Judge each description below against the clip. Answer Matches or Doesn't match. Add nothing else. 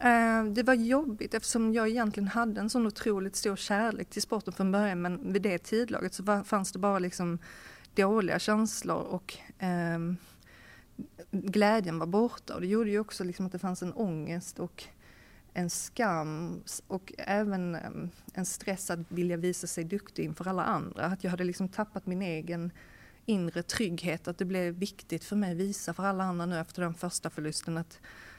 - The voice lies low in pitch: Doesn't match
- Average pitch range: Matches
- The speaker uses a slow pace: Doesn't match